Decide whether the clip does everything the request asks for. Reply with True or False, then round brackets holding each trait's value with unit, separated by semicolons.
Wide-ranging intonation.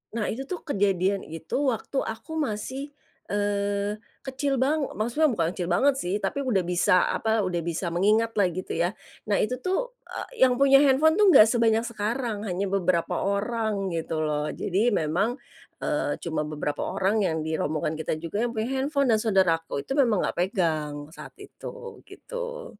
True (6.6 semitones)